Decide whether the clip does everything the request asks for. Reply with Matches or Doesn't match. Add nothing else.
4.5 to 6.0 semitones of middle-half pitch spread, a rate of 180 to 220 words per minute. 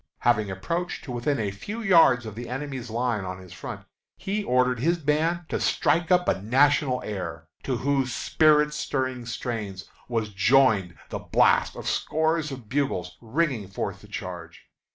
Doesn't match